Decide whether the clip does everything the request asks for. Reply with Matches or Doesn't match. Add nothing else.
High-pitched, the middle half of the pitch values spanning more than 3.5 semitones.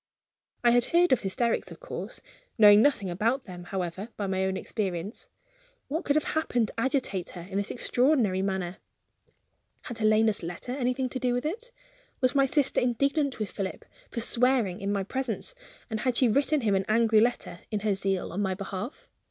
Matches